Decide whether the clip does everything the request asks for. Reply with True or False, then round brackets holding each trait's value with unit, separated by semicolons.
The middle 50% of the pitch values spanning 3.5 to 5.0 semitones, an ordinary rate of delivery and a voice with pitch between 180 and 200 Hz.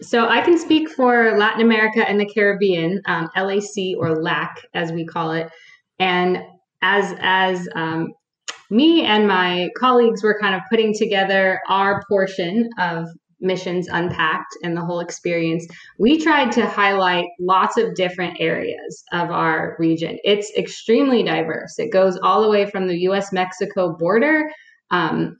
True (3.9 semitones; 155 wpm; 190 Hz)